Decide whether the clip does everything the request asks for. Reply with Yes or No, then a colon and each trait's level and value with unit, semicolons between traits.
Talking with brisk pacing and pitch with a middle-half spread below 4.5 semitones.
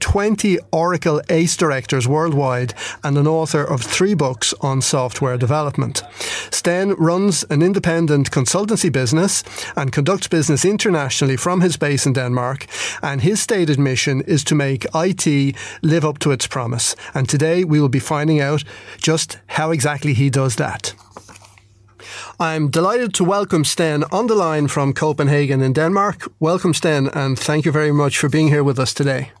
No: average, 165 wpm; average, 3.4 semitones